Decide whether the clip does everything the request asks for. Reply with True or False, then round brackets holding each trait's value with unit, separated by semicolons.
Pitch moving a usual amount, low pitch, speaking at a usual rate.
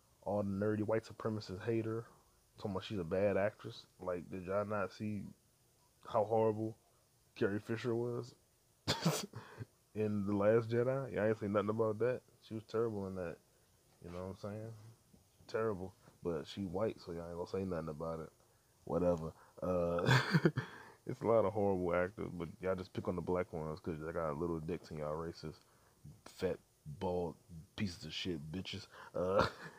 True (3.9 semitones; 100 Hz; 175 wpm)